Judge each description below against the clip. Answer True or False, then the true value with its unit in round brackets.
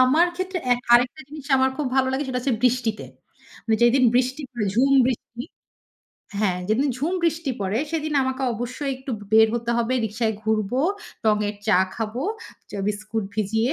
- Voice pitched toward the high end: True (245 Hz)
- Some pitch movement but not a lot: True (3.4 semitones)